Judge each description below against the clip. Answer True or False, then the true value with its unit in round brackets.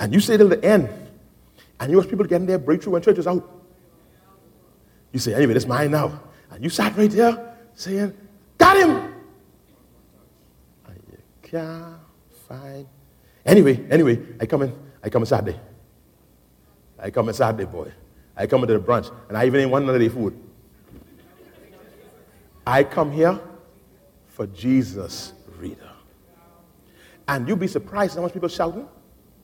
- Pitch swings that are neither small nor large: False (7.8 semitones)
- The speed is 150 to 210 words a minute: True (155 wpm)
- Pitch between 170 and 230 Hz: False (150 Hz)